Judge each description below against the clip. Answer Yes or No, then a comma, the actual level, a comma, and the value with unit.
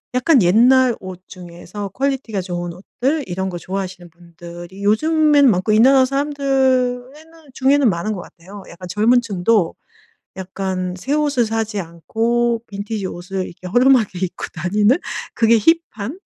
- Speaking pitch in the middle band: No, high, 215 Hz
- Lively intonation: Yes, wide, 6.0 semitones